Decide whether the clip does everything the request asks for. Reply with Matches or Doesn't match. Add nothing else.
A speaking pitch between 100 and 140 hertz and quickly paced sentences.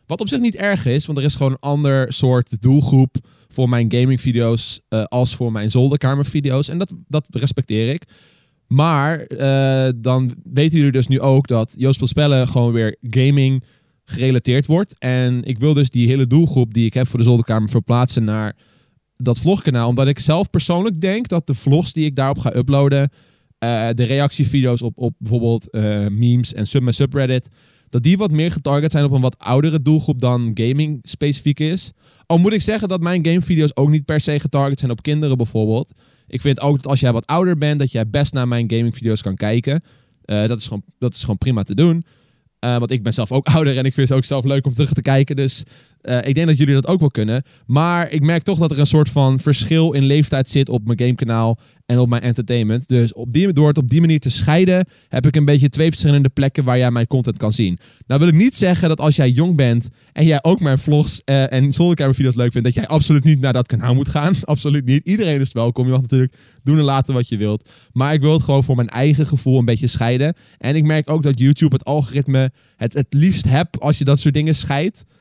Matches